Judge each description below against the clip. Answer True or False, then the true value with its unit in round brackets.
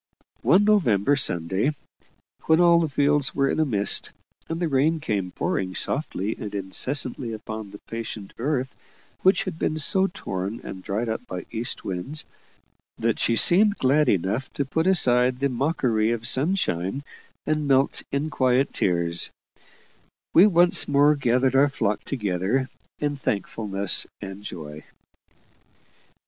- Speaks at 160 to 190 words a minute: False (140 wpm)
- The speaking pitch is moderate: False (130 Hz)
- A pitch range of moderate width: False (6.4 semitones)